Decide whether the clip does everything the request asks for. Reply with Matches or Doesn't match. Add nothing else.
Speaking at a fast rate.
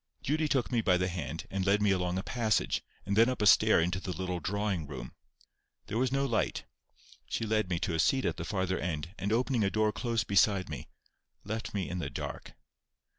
Matches